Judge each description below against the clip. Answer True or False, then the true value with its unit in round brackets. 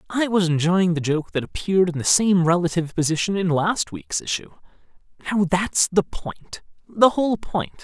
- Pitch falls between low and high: True (175 Hz)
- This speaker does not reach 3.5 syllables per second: False (5.1 syllables/s)